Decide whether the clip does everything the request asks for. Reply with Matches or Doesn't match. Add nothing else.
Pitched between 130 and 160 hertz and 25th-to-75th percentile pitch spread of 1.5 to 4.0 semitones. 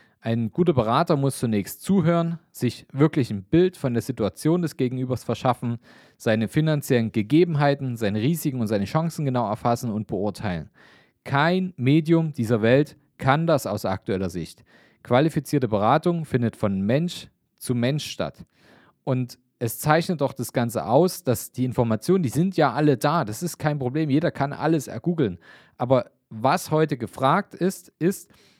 Doesn't match